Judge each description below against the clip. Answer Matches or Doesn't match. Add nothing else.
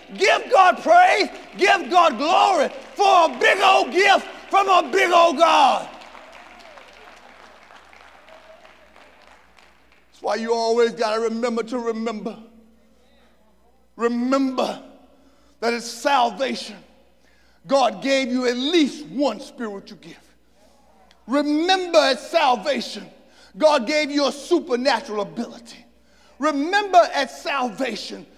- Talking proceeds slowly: Matches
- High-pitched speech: Matches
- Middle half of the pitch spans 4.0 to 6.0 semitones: Matches